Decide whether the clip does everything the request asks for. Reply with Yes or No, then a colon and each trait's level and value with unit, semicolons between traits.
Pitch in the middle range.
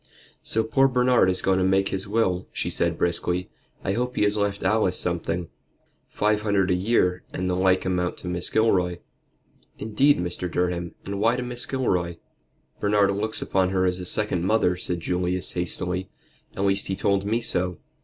No: very low, 95 Hz